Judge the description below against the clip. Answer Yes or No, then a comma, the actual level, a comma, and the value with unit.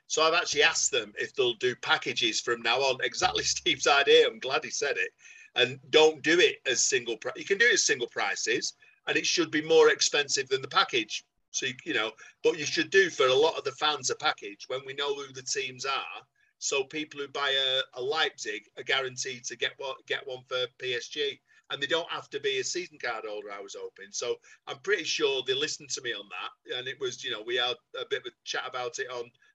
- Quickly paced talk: Yes, fast, 245 wpm